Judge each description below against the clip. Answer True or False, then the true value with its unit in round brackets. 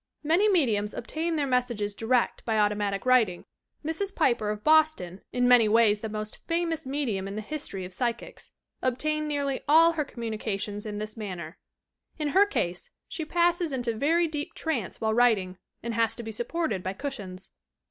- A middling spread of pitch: False (6.6 semitones)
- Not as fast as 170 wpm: False (175 wpm)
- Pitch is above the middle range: True (240 Hz)